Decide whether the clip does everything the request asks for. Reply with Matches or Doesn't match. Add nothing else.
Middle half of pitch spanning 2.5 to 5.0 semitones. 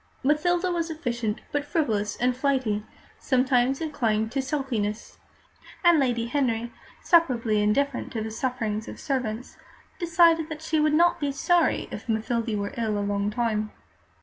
Doesn't match